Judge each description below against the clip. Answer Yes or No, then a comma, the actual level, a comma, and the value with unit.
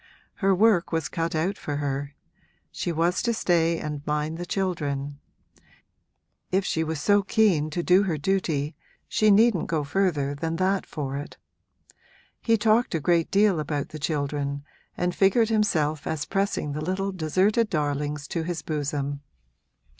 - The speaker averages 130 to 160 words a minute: Yes, average, 155 wpm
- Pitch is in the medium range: Yes, medium, 165 Hz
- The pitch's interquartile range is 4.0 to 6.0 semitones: Yes, average, 4.6 semitones